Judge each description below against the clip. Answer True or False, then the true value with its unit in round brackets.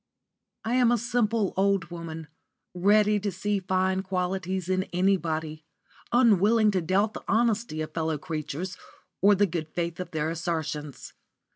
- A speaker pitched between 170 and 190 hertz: True (185 Hz)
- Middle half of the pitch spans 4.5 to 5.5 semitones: False (3.8 semitones)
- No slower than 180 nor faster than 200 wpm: False (150 wpm)